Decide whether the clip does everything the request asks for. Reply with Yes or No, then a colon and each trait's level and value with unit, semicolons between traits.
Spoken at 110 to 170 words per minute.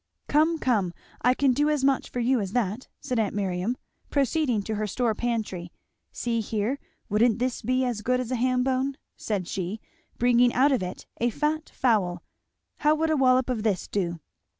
No: average, 190 wpm